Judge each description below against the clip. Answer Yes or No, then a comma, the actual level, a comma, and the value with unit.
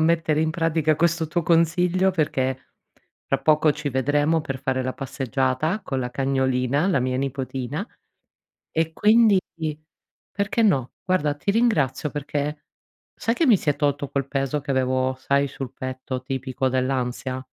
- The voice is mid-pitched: Yes, medium, 145 Hz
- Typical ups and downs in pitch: Yes, average, 3.8 semitones